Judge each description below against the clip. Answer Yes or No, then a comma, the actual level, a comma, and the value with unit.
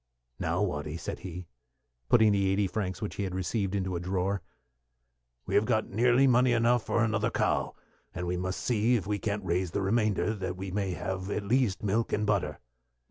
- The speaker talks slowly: No, average, 195 wpm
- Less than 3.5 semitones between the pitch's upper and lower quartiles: Yes, average, 3.0 semitones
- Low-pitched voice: Yes, low, 100 Hz